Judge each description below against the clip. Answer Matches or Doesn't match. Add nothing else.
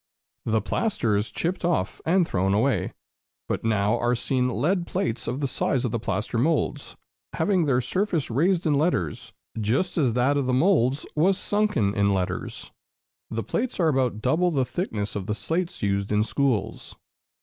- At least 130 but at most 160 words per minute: Doesn't match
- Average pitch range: Doesn't match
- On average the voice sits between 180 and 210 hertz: Doesn't match